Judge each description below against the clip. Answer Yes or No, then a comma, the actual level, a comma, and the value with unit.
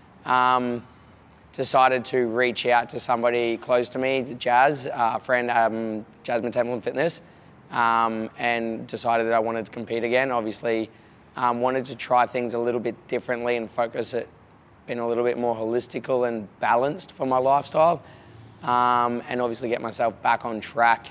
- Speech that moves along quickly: No, average, 170 wpm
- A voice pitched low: Yes, low, 120 Hz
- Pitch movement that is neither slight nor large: No, narrow, 1.3 semitones